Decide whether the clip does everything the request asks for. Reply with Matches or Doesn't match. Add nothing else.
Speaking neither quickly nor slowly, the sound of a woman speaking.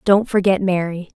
Matches